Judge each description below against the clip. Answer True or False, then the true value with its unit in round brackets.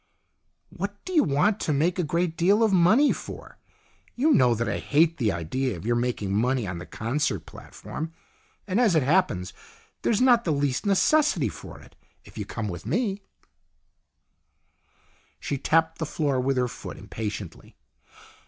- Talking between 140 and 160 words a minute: False (170 wpm)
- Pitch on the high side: False (150 Hz)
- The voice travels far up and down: True (8.2 semitones)